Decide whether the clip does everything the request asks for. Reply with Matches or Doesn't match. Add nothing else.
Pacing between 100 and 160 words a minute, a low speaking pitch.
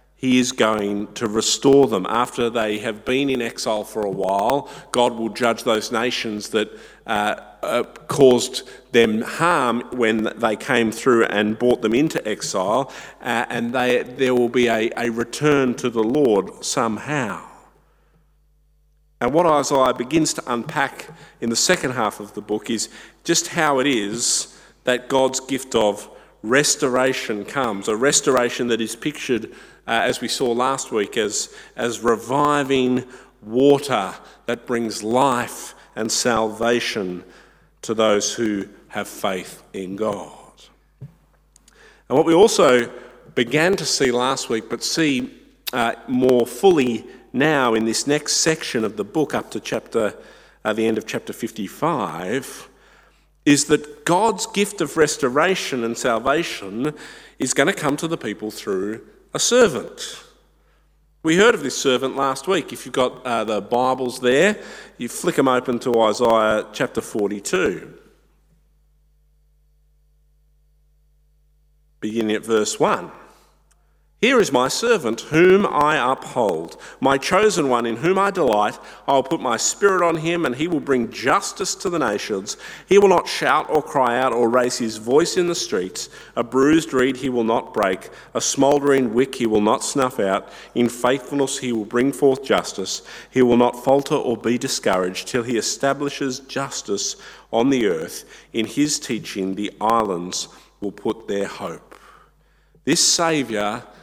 Matches